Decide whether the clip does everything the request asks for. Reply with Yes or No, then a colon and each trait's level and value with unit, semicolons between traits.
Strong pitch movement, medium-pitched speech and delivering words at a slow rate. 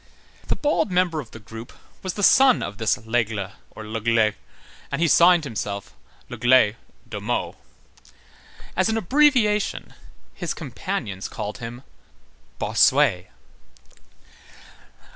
No: wide, 8.9 semitones; low, 130 Hz; slow, 115 wpm